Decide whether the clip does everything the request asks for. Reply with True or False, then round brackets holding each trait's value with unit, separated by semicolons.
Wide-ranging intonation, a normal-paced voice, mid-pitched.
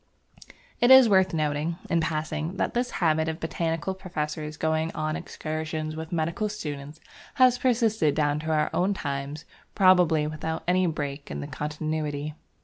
False (3.0 semitones; 150 wpm; 160 Hz)